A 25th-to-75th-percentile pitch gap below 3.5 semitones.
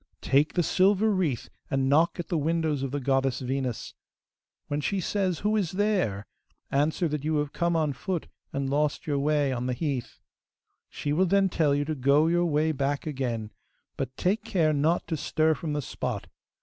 No: average, 3.9 semitones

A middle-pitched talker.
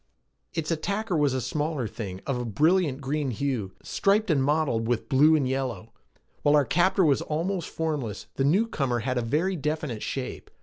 Yes: medium, 145 Hz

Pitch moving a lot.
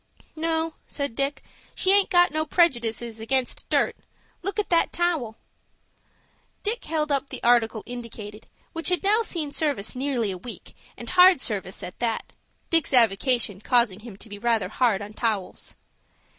Yes: wide, 6.8 semitones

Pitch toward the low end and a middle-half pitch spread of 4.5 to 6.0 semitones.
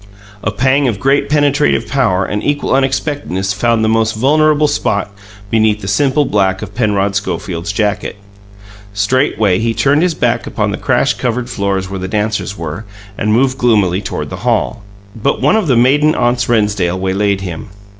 Yes: low, 110 Hz; average, 5.1 semitones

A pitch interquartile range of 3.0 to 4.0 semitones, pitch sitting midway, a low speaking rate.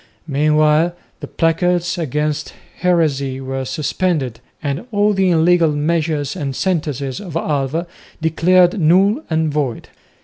Yes: average, 3.5 semitones; medium, 160 Hz; slow, 115 wpm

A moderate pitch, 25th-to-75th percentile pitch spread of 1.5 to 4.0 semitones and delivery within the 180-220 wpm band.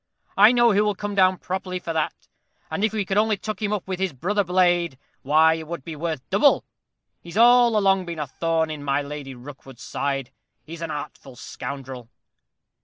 No: medium, 170 Hz; wide, 5.5 semitones; average, 195 wpm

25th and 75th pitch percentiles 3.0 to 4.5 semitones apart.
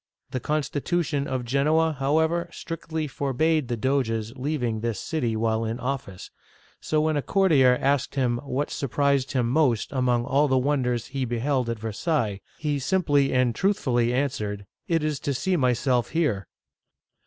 Yes: average, 4.0 semitones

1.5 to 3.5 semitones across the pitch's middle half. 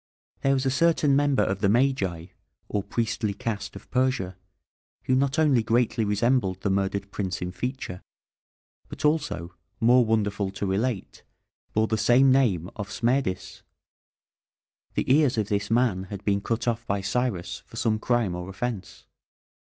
No: average, 4.6 semitones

